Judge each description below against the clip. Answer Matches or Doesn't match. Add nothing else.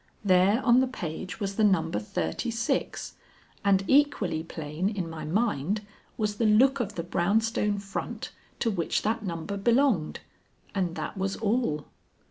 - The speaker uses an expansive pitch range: Doesn't match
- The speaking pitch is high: Matches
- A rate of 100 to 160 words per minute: Matches